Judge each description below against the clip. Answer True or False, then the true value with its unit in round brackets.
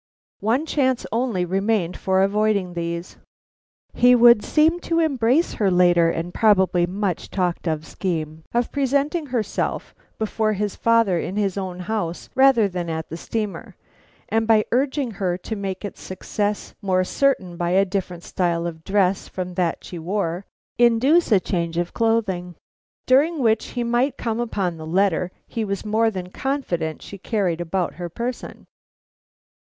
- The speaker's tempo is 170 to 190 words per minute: False (160 wpm)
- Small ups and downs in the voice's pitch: False (4.6 semitones)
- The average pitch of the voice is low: False (200 Hz)